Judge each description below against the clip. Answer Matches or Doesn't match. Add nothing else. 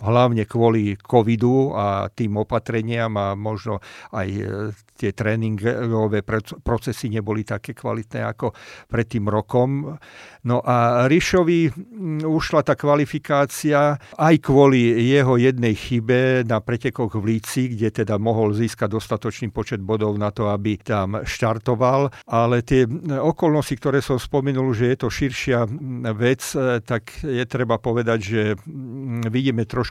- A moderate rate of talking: Matches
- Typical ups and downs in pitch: Matches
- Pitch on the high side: Doesn't match